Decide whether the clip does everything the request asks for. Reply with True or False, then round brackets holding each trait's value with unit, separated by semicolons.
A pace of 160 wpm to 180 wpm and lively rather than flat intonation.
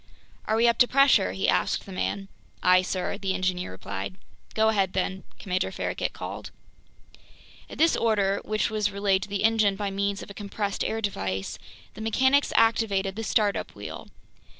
False (175 wpm; 2.4 semitones)